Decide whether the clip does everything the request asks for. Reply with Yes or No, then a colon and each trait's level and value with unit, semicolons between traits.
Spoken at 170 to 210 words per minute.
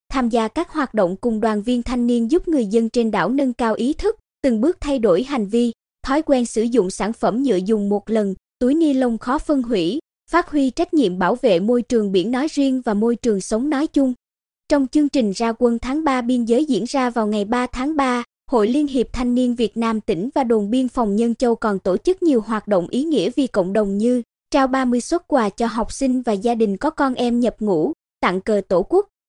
No: average, 245 wpm